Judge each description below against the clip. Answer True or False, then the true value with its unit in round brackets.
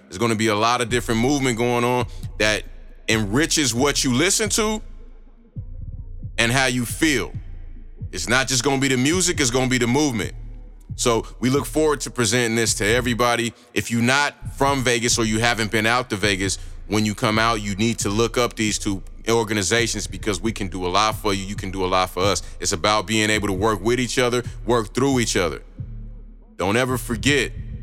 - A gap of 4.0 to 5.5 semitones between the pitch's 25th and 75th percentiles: False (2.8 semitones)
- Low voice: True (115 Hz)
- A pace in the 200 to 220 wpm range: True (205 wpm)